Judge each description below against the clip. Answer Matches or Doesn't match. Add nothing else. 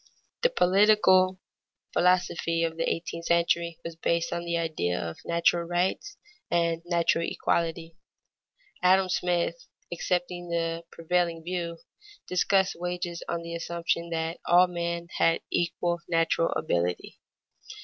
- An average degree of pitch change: Doesn't match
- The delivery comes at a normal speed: Doesn't match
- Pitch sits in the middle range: Matches